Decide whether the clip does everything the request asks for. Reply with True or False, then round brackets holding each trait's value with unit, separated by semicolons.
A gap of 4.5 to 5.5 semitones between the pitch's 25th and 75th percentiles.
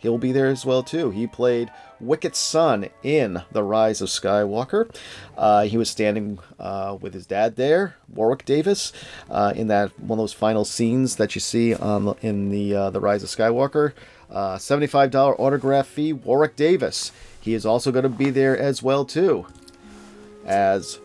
True (4.9 semitones)